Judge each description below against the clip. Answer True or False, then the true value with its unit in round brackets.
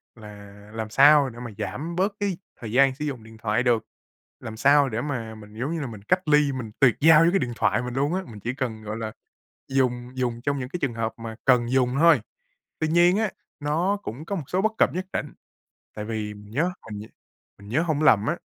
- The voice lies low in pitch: True (130 Hz)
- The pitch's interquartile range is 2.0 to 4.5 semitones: False (5.4 semitones)